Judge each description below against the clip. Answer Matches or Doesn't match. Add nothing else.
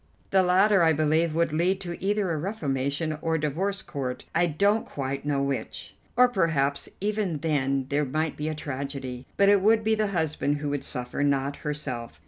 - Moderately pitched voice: Matches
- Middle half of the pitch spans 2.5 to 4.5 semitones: Doesn't match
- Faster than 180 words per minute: Matches